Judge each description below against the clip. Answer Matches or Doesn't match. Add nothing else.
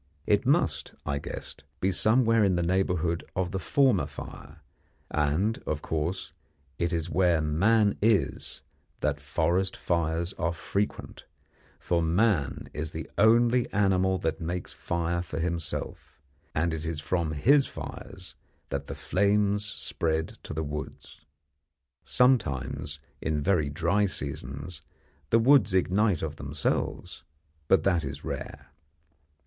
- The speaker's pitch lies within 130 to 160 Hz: Doesn't match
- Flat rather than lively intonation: Doesn't match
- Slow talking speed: Matches